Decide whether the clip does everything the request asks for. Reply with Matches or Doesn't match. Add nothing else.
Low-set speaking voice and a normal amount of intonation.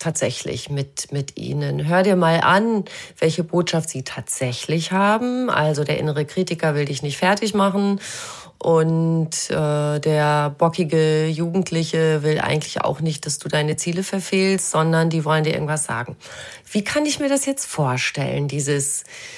Doesn't match